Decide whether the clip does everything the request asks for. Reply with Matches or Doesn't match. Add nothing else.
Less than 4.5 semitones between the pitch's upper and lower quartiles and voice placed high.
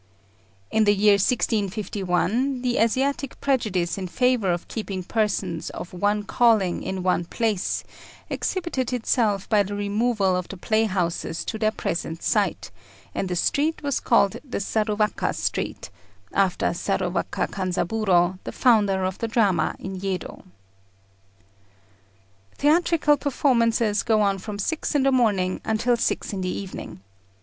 Matches